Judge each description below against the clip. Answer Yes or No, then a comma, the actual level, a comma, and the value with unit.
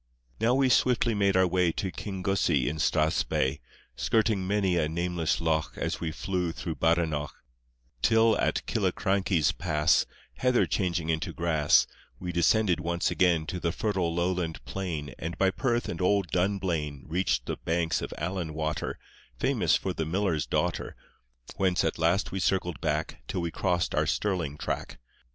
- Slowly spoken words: No, average, 155 wpm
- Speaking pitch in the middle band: No, very low, 85 Hz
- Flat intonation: No, average, 3.2 semitones